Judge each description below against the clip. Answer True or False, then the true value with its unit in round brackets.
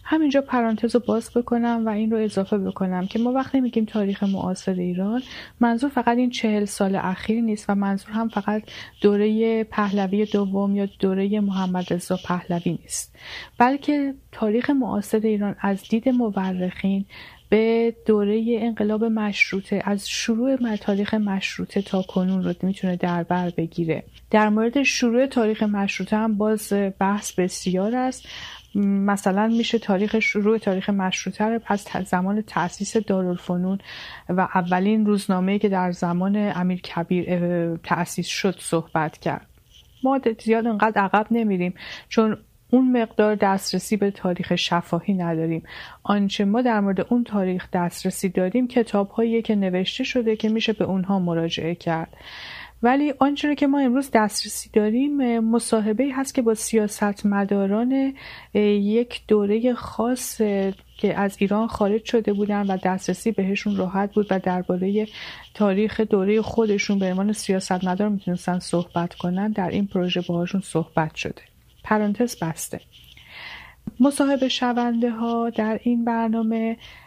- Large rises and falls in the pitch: False (3.2 semitones)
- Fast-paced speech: False (135 wpm)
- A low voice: False (205 Hz)